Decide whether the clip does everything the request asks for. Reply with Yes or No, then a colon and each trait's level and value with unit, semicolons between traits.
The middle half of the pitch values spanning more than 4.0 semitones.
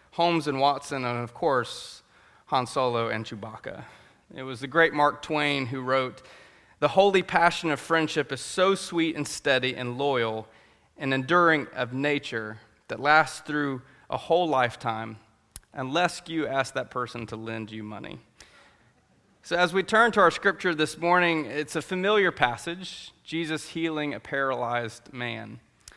Yes: average, 5.3 semitones